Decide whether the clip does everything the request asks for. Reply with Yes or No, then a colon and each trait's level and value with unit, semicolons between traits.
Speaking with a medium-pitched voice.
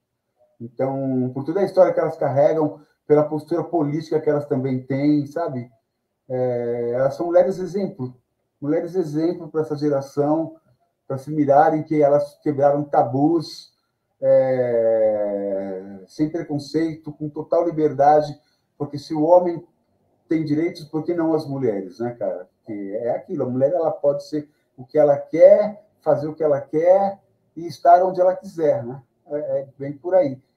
Yes: medium, 150 Hz